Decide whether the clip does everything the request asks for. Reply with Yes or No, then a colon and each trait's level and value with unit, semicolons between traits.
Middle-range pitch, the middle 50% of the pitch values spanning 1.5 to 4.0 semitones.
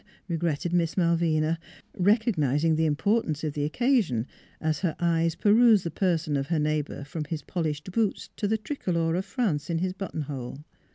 Yes: medium, 165 Hz; average, 3.7 semitones